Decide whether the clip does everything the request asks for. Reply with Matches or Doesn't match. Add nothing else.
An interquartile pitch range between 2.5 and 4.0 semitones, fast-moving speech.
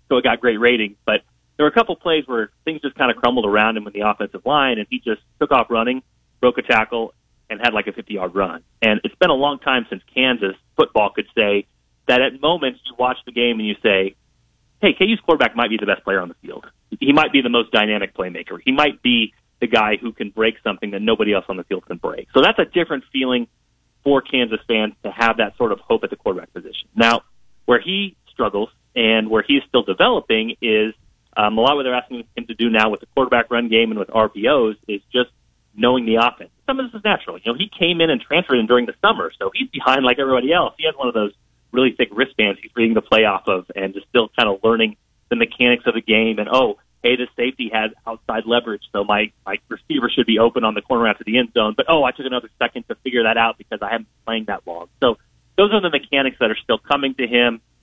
Matches